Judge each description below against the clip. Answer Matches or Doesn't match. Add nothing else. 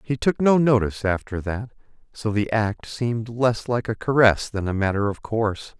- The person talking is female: Doesn't match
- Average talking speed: Matches